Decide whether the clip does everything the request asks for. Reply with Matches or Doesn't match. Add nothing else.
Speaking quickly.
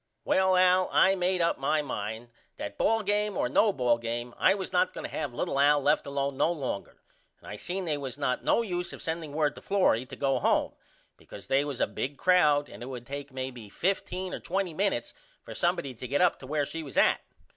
Matches